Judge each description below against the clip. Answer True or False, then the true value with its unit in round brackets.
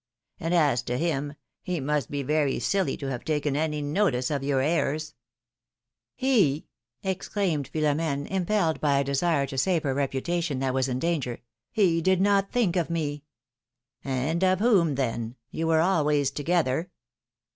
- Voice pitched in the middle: True (150 Hz)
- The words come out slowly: False (150 wpm)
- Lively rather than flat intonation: False (4.2 semitones)